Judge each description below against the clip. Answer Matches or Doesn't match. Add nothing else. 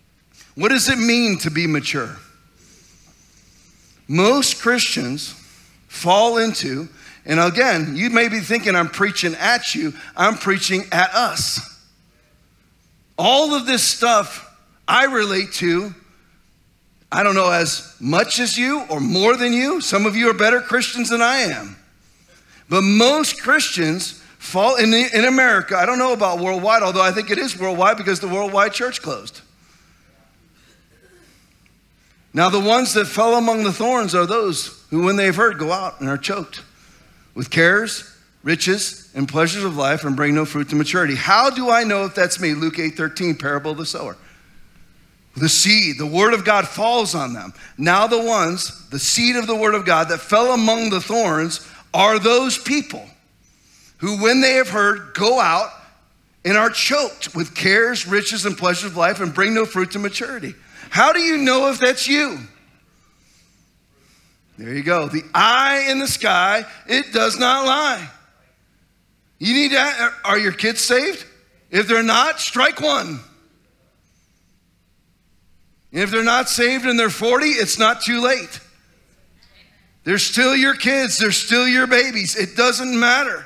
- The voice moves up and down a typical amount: Doesn't match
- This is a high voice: Matches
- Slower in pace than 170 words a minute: Matches